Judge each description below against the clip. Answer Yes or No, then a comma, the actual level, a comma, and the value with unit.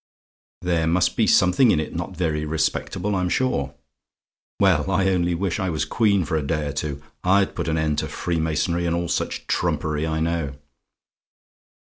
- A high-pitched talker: No, very low, 85 Hz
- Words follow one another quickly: No, average, 175 wpm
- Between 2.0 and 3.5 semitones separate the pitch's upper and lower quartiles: Yes, average, 2.9 semitones